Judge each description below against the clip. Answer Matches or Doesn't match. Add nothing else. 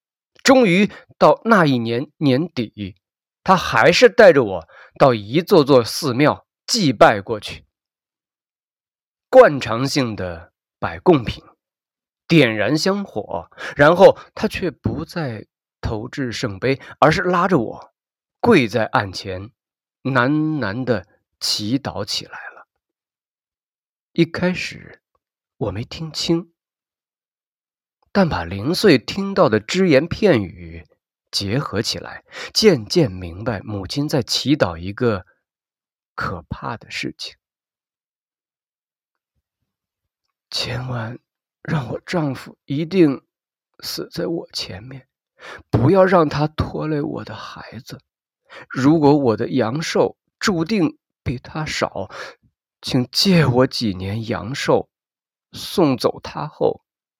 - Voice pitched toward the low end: Matches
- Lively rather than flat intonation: Matches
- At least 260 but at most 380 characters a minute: Doesn't match